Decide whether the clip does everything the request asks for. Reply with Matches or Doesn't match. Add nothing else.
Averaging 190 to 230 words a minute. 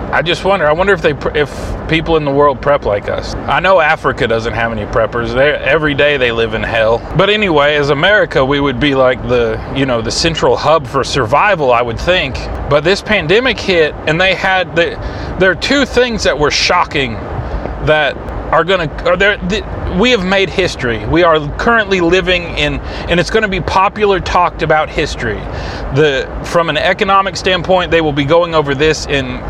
Matches